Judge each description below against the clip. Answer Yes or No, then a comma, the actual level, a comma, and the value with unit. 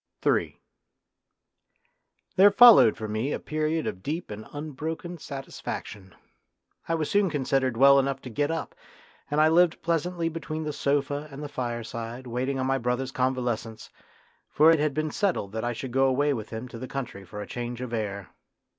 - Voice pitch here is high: No, low, 135 Hz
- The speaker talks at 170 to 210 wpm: Yes, average, 180 wpm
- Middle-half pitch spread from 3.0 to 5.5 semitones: Yes, average, 4.6 semitones